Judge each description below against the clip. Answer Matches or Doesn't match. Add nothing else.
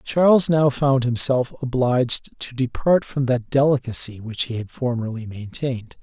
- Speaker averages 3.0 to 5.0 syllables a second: Matches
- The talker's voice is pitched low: Matches